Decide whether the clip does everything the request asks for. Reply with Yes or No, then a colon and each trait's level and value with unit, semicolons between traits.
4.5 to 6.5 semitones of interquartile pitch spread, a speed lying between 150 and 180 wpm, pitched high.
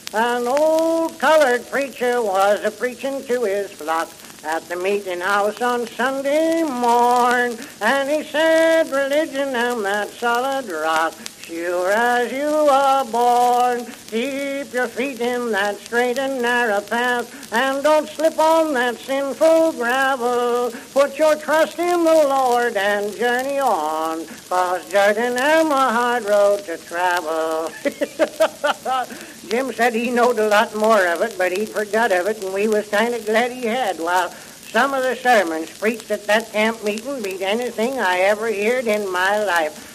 Yes: average, 4.8 semitones; average, 155 wpm; high, 240 Hz